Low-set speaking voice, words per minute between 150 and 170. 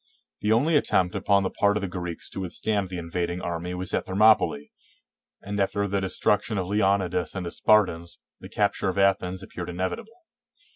No: very low, 95 Hz; average, 185 wpm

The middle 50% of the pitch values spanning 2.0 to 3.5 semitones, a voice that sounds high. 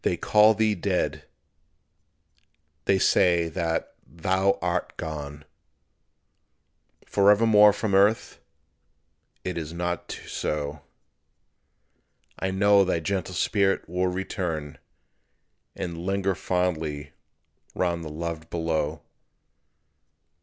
No: average, 3.2 semitones; very low, 90 Hz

